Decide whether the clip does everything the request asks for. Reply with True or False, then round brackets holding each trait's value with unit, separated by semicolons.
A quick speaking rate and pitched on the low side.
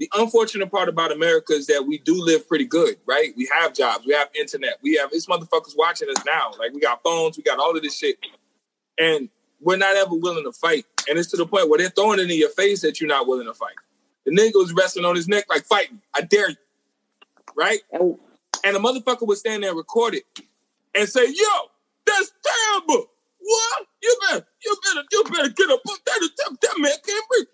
False (220 wpm; 265 Hz)